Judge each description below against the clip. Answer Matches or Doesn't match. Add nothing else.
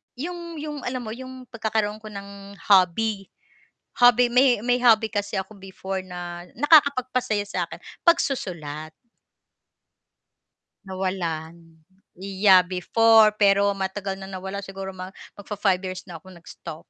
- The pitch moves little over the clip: Doesn't match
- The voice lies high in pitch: Matches